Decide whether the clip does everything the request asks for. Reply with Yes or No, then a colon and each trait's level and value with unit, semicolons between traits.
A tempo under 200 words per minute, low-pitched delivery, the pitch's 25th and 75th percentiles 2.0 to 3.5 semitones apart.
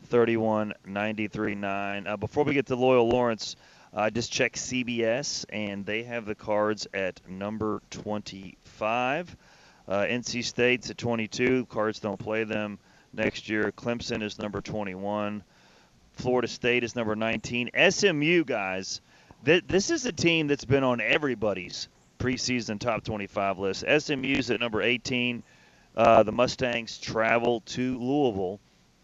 Yes: average, 140 wpm; low, 115 Hz; average, 3.0 semitones